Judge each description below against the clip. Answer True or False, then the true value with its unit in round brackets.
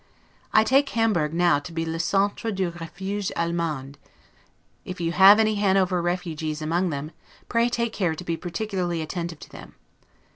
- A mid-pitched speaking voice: True (175 Hz)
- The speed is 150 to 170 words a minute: True (160 wpm)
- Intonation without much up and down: False (3.4 semitones)